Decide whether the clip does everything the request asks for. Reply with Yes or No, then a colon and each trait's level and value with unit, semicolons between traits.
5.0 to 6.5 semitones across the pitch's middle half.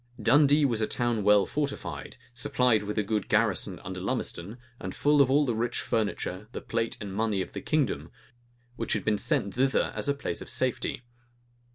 No: average, 4.4 semitones